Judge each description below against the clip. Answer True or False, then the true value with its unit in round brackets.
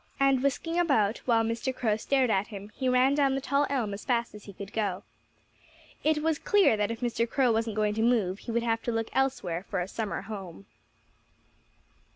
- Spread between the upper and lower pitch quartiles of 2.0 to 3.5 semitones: False (4.3 semitones)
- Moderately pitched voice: False (230 Hz)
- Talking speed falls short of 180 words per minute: False (205 wpm)